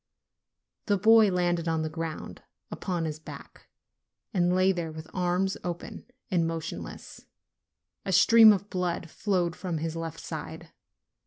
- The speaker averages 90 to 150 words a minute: Yes, average, 140 wpm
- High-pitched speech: No, medium, 175 Hz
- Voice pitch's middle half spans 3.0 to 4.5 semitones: No, narrow, 2.5 semitones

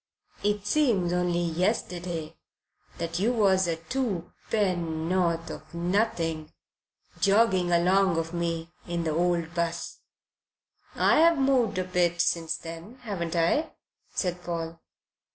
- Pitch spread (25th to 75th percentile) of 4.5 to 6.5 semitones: No, average, 3.0 semitones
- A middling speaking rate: No, slow, 115 wpm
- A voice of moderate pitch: Yes, medium, 175 Hz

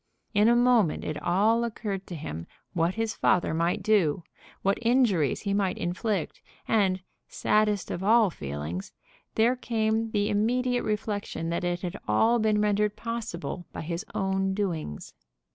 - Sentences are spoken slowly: No, average, 150 wpm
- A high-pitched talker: Yes, high, 205 Hz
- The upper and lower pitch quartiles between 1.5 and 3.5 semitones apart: No, average, 4.1 semitones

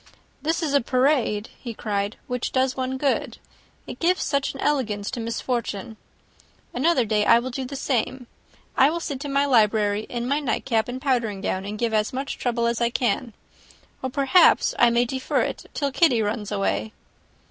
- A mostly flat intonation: No, average, 3.7 semitones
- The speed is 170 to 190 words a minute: Yes, average, 185 wpm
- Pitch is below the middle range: No, high, 245 Hz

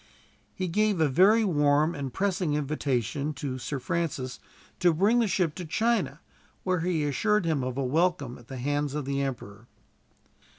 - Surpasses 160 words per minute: Yes, average, 170 wpm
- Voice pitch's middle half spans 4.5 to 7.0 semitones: Yes, average, 4.9 semitones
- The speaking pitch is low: No, medium, 150 Hz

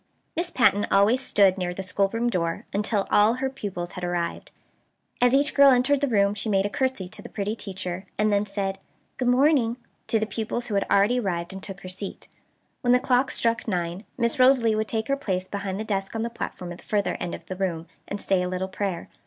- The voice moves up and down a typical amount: Yes, average, 4.1 semitones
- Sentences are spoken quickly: Yes, fast, 225 wpm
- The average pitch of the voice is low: No, high, 205 Hz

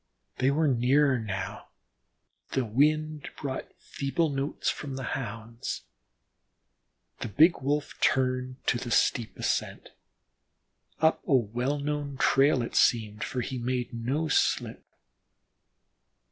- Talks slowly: Yes, slow, 120 wpm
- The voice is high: No, low, 130 Hz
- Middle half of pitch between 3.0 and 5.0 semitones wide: Yes, average, 3.4 semitones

